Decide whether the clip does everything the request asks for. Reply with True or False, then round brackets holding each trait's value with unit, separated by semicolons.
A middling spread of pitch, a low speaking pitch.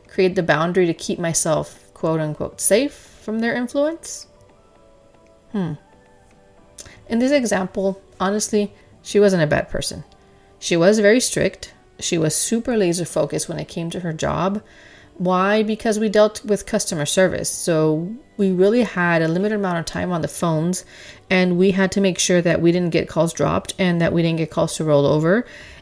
False (4.2 semitones; 180 Hz)